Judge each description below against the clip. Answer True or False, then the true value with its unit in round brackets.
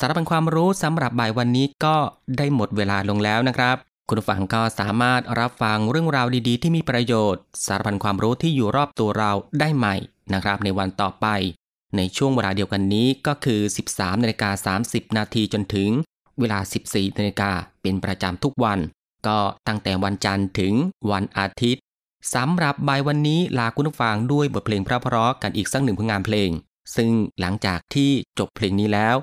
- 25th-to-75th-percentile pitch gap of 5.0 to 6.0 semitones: False (4.4 semitones)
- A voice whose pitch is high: False (110 Hz)